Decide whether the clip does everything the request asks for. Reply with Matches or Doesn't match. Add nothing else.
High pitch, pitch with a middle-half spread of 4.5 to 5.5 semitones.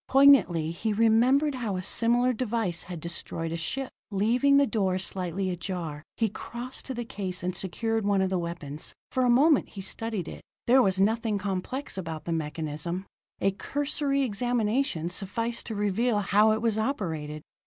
Matches